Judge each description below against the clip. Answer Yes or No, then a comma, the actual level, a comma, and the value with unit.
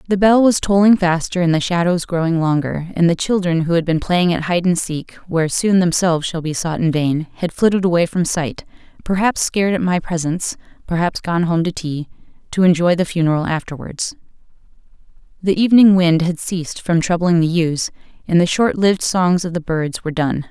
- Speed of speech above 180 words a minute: Yes, average, 195 wpm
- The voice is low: No, medium, 175 Hz